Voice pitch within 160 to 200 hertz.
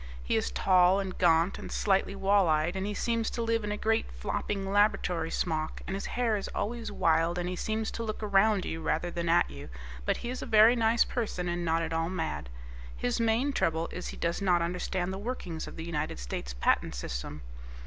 Yes: medium, 185 Hz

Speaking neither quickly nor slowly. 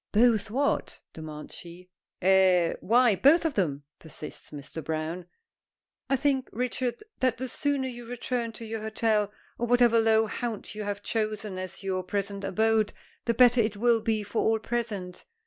Yes: average, 165 wpm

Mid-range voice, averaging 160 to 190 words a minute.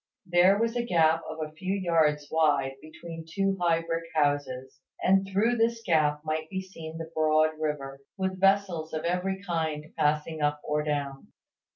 Yes: medium, 160 Hz; average, 170 wpm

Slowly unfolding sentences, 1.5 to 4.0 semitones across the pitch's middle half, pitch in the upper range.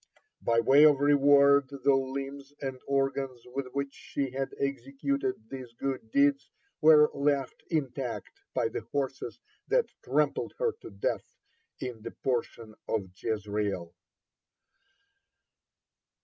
No: slow, 120 wpm; average, 2.8 semitones; low, 135 Hz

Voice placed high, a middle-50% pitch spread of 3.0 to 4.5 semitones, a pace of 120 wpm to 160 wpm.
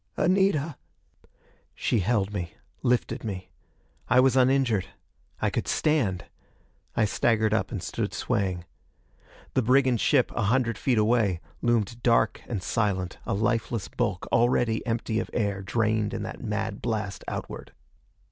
No: low, 115 Hz; average, 3.3 semitones; average, 140 wpm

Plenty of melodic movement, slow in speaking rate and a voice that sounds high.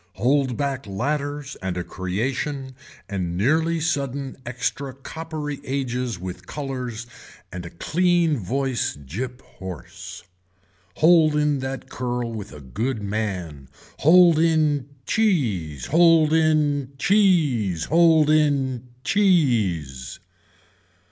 No: wide, 6.8 semitones; slow, 105 wpm; low, 135 Hz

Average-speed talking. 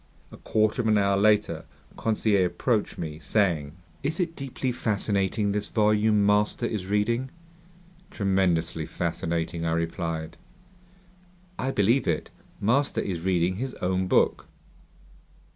No: slow, 125 wpm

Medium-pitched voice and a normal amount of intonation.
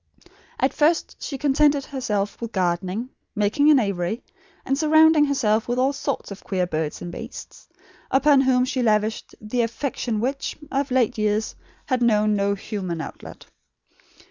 No: high, 235 Hz; average, 4.8 semitones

